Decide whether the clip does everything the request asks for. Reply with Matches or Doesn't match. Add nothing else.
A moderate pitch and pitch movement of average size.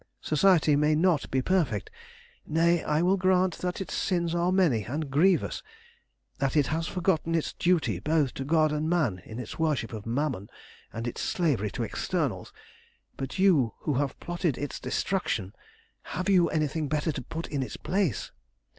Matches